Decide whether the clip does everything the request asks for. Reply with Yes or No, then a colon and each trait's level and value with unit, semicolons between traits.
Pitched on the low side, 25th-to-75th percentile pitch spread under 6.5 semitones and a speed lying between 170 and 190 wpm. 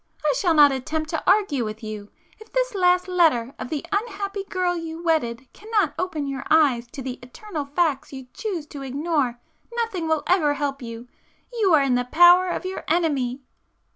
No: very high, 315 Hz; wide, 5.5 semitones; average, 185 wpm